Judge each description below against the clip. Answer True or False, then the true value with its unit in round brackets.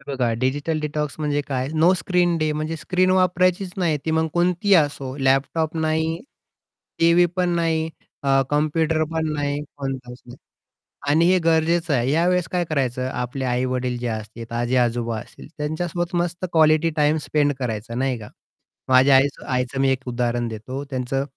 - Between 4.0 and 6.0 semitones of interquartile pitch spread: True (4.3 semitones)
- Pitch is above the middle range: False (150 Hz)